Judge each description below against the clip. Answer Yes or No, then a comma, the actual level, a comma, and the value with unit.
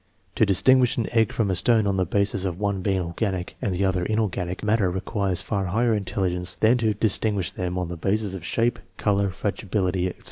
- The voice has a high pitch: No, low, 100 Hz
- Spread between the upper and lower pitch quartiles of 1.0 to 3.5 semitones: Yes, average, 2.8 semitones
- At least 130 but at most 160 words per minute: No, average, 200 wpm